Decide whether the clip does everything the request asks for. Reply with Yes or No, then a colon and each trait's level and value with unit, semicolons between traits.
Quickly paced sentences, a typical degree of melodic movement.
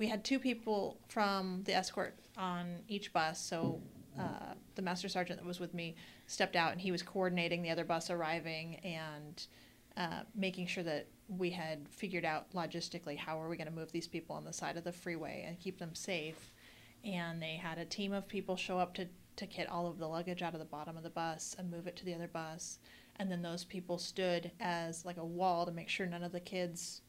No: fast, 230 wpm; narrow, 2.1 semitones